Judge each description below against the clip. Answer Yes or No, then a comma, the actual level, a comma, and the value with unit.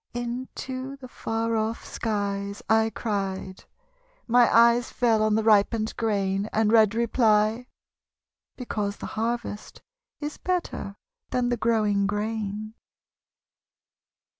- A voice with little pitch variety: Yes, narrow, 2.3 semitones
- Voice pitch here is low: No, high, 220 Hz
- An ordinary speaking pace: No, slow, 110 wpm